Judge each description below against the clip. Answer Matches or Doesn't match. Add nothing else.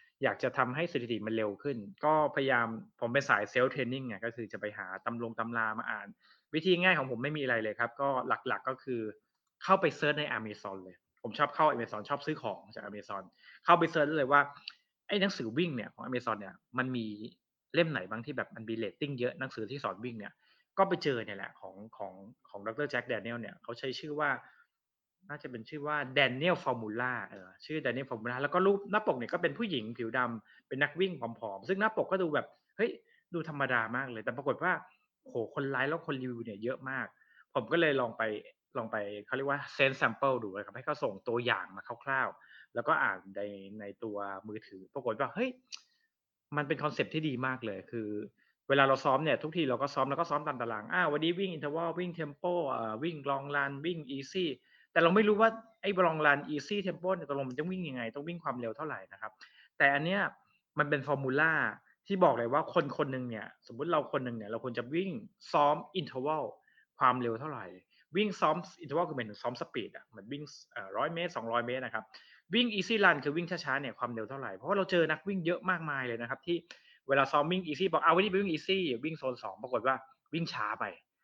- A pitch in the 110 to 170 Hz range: Matches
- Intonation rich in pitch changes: Matches